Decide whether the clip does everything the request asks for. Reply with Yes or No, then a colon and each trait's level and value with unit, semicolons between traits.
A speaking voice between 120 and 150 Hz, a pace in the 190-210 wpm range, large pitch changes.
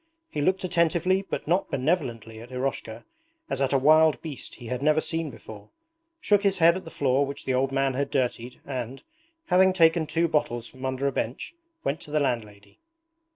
No: medium, 140 Hz; average, 195 wpm; average, 4.5 semitones